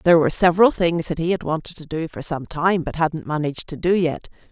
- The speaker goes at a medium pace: No, fast, 255 wpm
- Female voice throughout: Yes, female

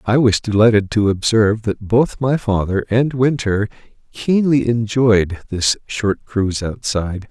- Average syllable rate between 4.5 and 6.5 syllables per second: No, 4.3 syllables/s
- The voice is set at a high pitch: No, low, 110 Hz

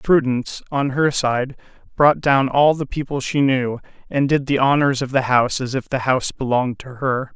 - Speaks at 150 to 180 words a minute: No, fast, 205 wpm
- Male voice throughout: Yes, male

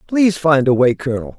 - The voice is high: No, medium, 150 Hz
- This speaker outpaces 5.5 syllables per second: Yes, 6.4 syllables/s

